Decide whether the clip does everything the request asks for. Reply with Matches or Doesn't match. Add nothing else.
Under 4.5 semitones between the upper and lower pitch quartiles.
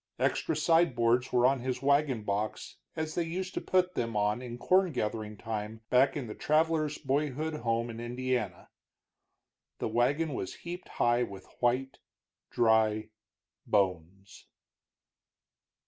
Doesn't match